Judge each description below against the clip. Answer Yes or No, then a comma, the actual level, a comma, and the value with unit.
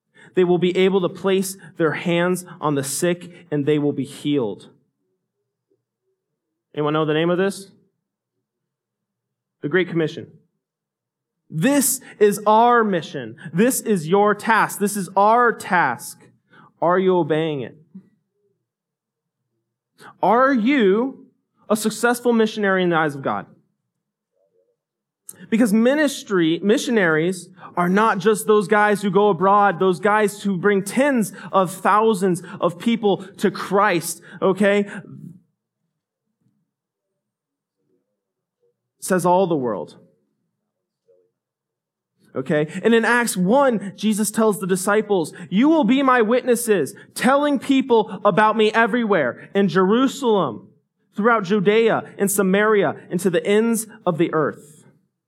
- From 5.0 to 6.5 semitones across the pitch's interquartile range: No, average, 4.0 semitones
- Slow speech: Yes, slow, 120 wpm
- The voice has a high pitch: Yes, high, 200 Hz